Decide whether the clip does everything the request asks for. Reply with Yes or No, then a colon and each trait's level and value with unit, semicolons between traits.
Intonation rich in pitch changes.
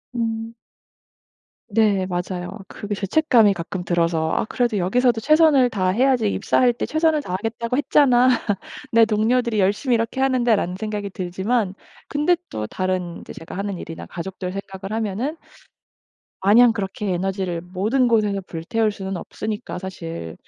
No: average, 4.4 semitones